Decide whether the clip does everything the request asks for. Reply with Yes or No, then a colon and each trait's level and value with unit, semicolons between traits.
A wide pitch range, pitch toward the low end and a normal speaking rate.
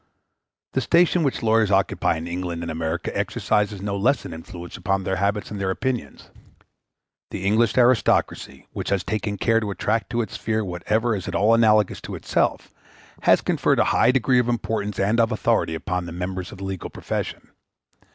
No: average, 3.4 semitones; low, 105 Hz; average, 185 wpm